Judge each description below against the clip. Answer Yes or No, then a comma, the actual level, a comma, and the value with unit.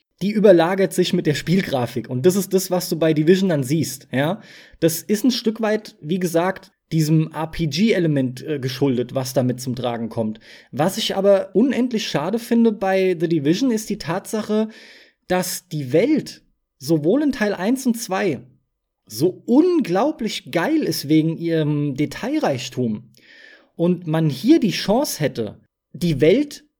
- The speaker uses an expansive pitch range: Yes, wide, 5.9 semitones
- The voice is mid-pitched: Yes, medium, 180 Hz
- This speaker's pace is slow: No, average, 150 wpm